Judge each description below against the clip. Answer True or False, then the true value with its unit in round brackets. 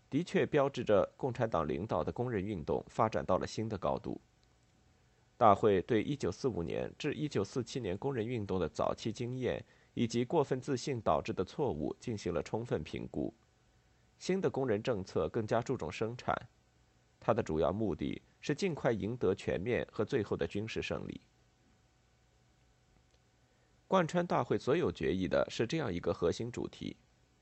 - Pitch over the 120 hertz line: False (115 Hz)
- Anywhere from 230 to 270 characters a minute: True (250 characters per minute)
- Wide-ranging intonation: True (6.5 semitones)